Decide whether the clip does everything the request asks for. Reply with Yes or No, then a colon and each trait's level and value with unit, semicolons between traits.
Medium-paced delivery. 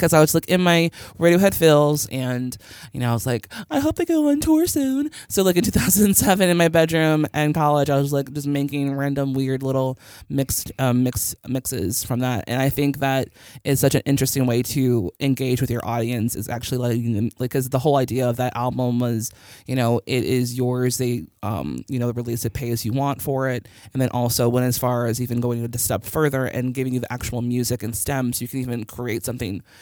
No: fast, 230 wpm